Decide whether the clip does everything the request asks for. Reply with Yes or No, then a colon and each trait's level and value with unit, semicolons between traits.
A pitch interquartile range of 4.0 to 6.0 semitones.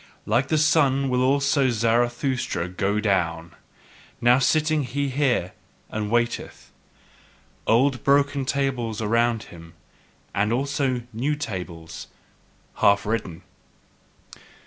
Yes: average, 4.7 semitones